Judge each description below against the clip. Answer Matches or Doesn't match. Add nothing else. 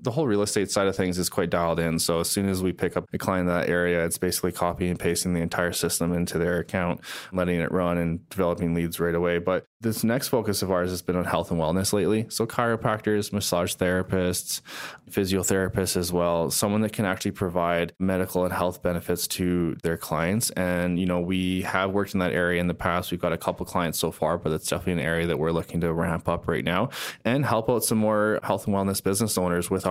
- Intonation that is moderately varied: Doesn't match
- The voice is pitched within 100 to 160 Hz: Doesn't match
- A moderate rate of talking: Doesn't match